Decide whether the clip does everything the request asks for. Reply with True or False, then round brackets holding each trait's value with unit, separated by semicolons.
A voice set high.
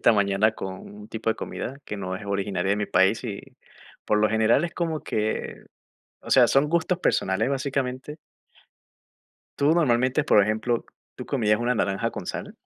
False (110 Hz)